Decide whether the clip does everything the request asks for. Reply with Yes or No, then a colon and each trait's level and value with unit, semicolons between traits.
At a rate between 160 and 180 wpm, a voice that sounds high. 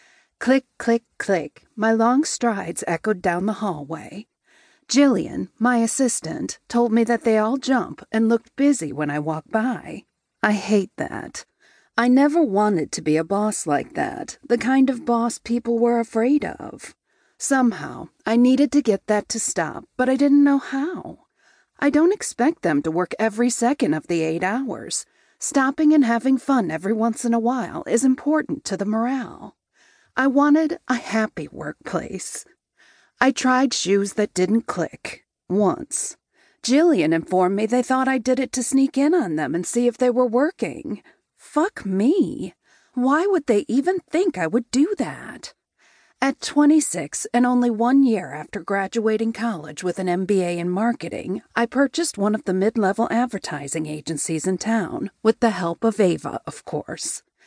Yes: average, 165 wpm; high, 235 Hz